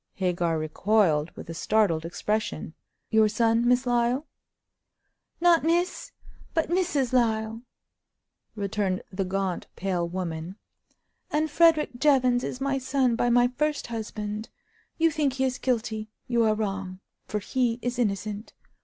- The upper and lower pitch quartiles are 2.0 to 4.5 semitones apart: No, average, 4.9 semitones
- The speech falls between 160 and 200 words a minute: No, slow, 135 wpm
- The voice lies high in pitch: Yes, high, 225 Hz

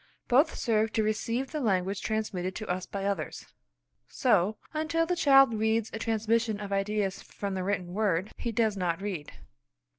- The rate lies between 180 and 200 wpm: No, average, 170 wpm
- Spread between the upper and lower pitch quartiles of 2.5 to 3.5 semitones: Yes, average, 2.8 semitones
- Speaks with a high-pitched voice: Yes, high, 215 Hz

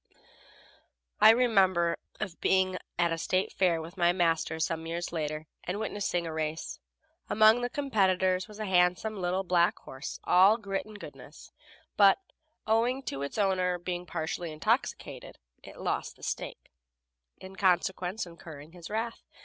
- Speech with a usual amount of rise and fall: Yes, average, 3.4 semitones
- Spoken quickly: No, average, 150 wpm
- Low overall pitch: No, medium, 185 Hz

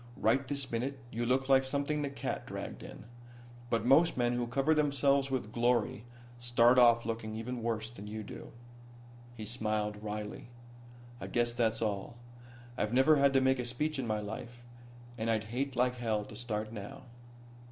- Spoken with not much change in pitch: No, average, 3.2 semitones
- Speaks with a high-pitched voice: No, low, 120 Hz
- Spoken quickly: No, average, 175 wpm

